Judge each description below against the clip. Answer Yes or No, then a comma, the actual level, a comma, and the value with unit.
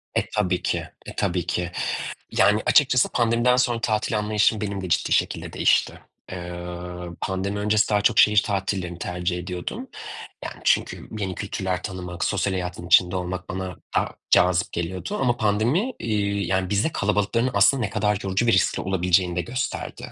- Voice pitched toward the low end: Yes, low, 100 Hz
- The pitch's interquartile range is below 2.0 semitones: No, average, 2.9 semitones